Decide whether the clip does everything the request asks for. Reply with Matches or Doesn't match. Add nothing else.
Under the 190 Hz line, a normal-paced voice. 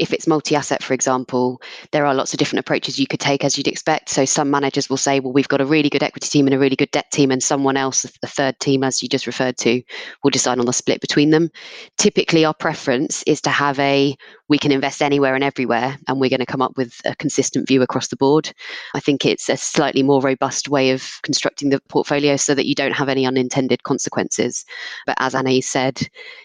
Doesn't match